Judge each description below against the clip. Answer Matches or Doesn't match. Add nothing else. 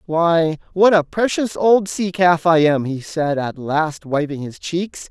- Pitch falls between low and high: Matches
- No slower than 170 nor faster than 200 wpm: Matches